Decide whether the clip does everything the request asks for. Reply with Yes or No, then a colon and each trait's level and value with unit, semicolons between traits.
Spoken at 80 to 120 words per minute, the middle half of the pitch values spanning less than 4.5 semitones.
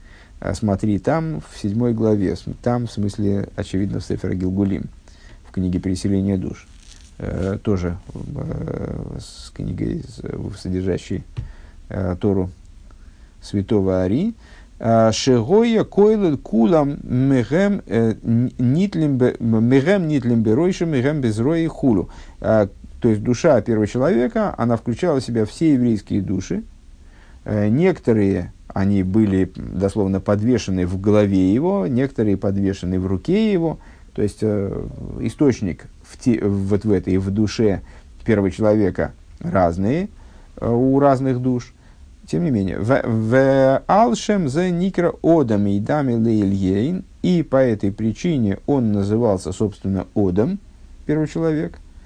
No: slow, 110 wpm; wide, 5.6 semitones